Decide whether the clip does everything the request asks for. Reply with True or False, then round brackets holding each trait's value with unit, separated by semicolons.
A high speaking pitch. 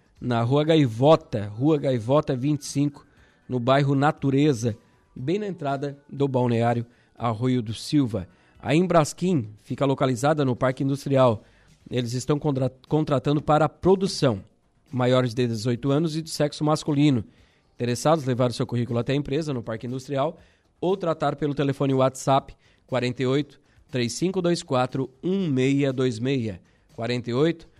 False (135 Hz)